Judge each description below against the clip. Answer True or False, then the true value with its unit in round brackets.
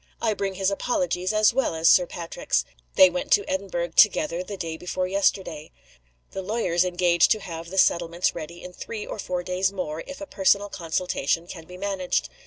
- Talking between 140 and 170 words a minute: False (190 wpm)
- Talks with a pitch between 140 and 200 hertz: True (185 Hz)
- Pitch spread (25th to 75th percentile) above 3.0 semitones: False (2.5 semitones)